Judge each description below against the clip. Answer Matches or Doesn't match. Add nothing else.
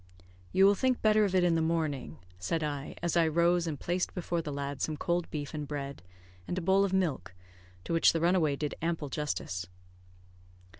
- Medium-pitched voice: Matches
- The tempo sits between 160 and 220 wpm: Matches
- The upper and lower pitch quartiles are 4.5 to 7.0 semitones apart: Doesn't match